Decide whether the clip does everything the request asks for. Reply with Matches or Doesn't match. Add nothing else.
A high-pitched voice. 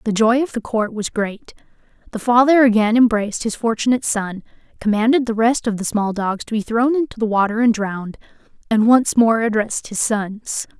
Matches